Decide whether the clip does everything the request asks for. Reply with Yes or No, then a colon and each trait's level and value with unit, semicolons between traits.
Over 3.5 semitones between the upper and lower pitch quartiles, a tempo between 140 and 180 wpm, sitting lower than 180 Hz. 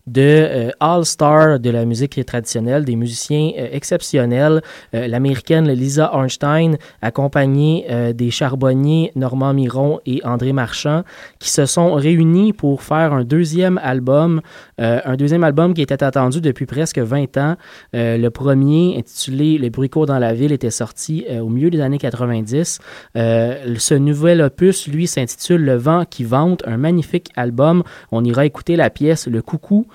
Yes: average, 4.2 semitones; average, 165 wpm; medium, 140 Hz